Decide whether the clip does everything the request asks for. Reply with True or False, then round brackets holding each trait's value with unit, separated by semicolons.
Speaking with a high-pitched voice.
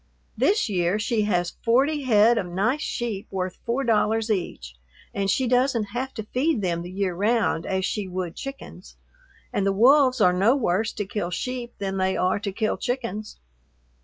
True (210 Hz)